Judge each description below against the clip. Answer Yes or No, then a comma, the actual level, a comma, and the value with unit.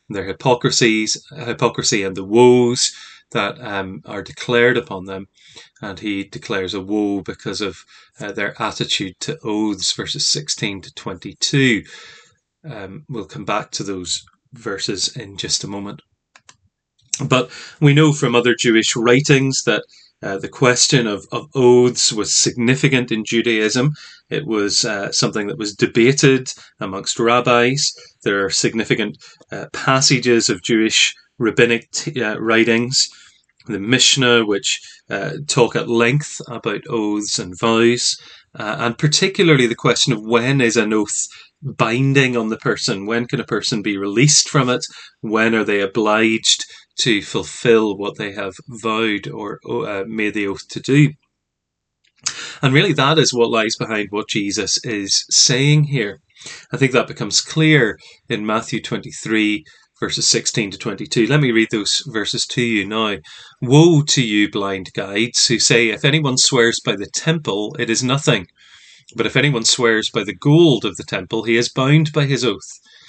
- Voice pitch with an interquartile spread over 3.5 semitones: Yes, average, 3.9 semitones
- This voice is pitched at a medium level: No, low, 120 Hz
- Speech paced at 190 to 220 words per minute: No, average, 155 wpm